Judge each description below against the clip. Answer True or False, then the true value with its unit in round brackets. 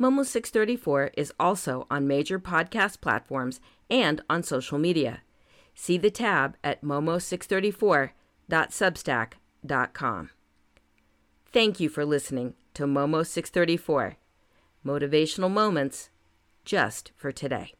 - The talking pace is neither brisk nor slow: False (100 wpm)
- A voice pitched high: False (155 Hz)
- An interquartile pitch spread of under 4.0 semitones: False (5.5 semitones)